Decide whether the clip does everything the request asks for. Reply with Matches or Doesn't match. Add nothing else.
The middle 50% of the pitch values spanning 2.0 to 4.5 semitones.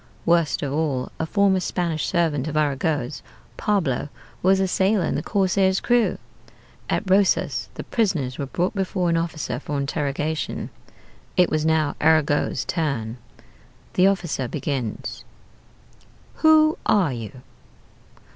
Doesn't match